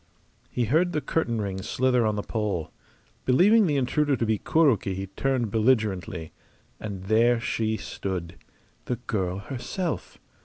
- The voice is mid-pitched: No, low, 115 Hz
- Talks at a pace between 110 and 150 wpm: Yes, average, 145 wpm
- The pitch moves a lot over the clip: No, average, 4.9 semitones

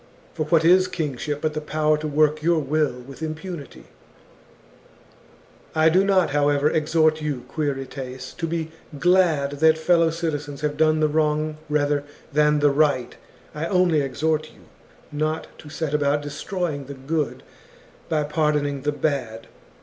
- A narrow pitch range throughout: Yes, narrow, 1.7 semitones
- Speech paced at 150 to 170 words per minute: Yes, average, 155 wpm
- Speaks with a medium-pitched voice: Yes, medium, 150 Hz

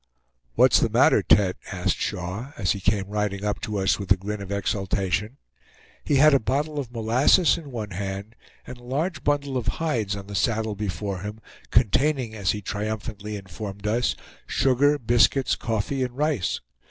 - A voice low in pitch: Yes, low, 110 Hz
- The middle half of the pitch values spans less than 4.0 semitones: No, average, 4.6 semitones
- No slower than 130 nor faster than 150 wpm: No, average, 175 wpm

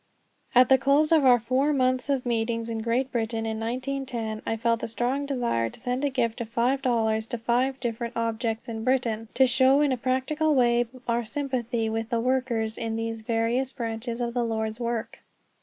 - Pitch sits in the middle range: No, high, 240 Hz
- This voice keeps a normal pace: Yes, average, 195 wpm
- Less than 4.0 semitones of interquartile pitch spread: Yes, narrow, 2.4 semitones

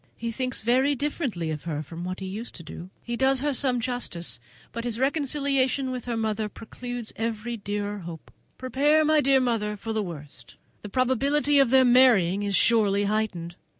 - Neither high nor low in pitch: No, high, 230 Hz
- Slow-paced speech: No, average, 185 wpm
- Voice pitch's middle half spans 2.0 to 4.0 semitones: No, average, 4.5 semitones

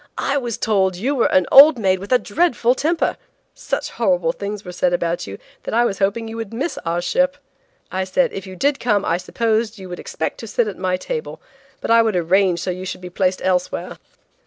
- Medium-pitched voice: No, high, 205 Hz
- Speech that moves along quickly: Yes, fast, 230 wpm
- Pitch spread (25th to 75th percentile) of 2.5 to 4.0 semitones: No, average, 4.6 semitones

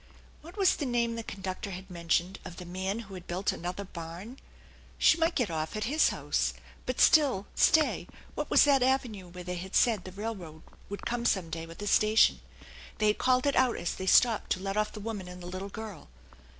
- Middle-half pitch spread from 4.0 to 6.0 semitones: Yes, average, 4.8 semitones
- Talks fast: Yes, fast, 215 wpm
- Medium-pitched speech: No, high, 200 Hz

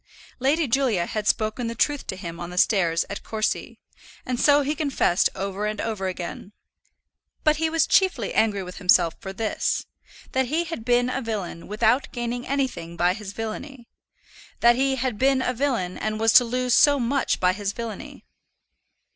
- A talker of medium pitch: No, high, 230 Hz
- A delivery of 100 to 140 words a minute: No, average, 180 wpm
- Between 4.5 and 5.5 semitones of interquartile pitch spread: Yes, average, 5.1 semitones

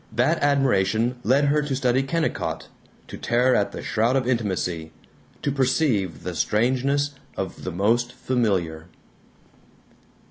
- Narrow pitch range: No, average, 5.2 semitones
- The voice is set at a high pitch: No, low, 120 Hz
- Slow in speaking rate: Yes, slow, 130 wpm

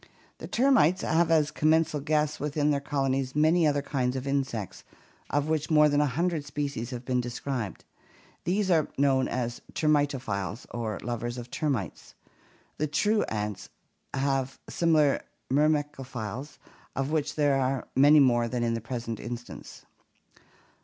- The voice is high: No, medium, 140 Hz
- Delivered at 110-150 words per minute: Yes, average, 145 wpm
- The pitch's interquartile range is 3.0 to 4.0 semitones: Yes, average, 3.6 semitones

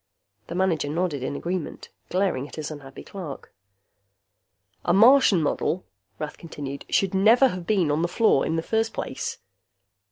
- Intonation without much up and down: No, average, 4.7 semitones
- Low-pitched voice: No, medium, 175 Hz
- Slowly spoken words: No, average, 155 wpm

